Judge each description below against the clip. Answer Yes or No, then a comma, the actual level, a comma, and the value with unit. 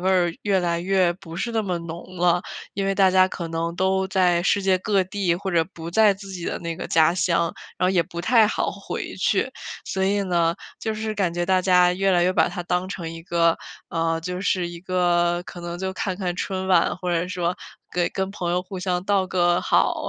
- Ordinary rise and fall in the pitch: No, narrow, 1.7 semitones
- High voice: No, medium, 180 Hz